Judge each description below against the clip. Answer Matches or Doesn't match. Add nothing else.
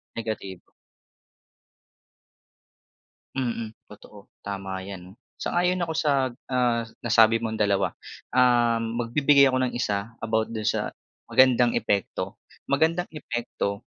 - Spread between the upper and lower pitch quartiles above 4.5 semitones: Doesn't match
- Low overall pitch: Matches